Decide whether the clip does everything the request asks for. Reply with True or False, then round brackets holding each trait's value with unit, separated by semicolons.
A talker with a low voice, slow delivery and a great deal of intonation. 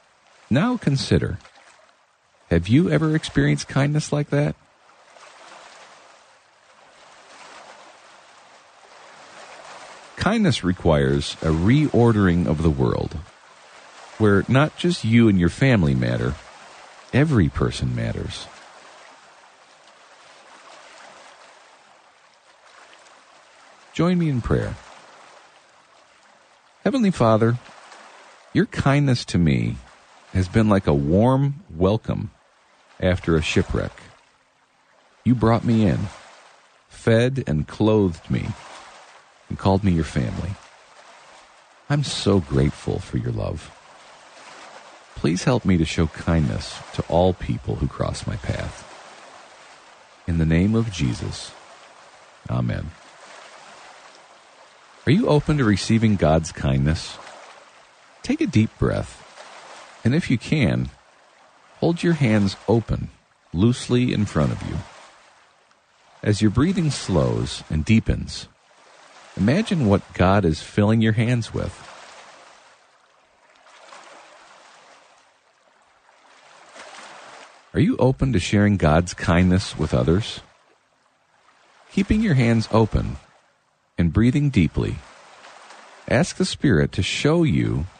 True (105 Hz; 100 wpm; 7.2 semitones)